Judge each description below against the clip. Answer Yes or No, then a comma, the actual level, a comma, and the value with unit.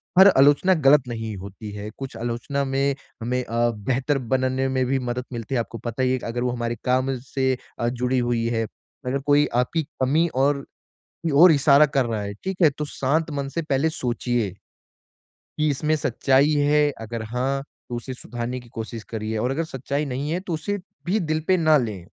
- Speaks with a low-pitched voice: Yes, low, 130 Hz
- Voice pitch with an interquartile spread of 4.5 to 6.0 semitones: No, average, 3.6 semitones